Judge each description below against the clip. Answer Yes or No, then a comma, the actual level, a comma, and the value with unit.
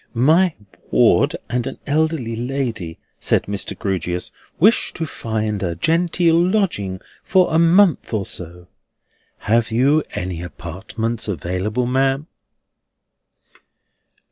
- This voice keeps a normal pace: No, slow, 110 wpm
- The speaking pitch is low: Yes, low, 115 Hz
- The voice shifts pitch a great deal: Yes, wide, 8.7 semitones